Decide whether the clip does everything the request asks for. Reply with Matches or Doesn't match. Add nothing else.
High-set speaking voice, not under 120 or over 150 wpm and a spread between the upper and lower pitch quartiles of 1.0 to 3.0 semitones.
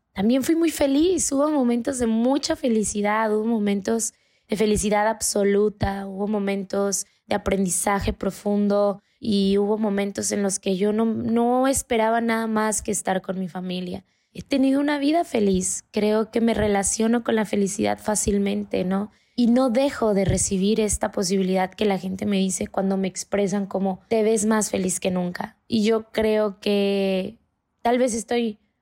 Doesn't match